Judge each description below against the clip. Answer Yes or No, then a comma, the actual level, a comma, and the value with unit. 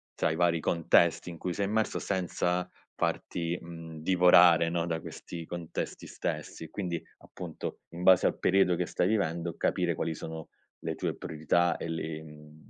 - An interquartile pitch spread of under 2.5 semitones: Yes, narrow, 1.7 semitones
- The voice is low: Yes, very low, 85 Hz